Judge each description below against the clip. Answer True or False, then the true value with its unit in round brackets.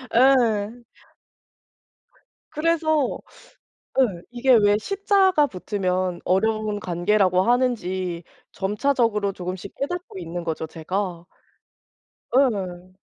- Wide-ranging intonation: True (6.0 semitones)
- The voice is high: True (205 Hz)